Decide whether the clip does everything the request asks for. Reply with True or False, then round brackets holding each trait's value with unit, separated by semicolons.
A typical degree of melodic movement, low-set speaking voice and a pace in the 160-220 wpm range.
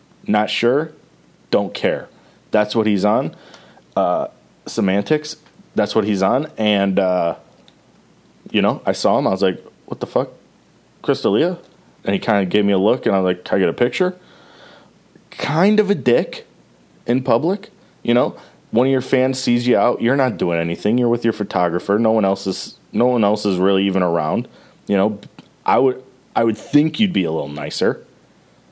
True (5.0 semitones; 115 Hz; 190 wpm)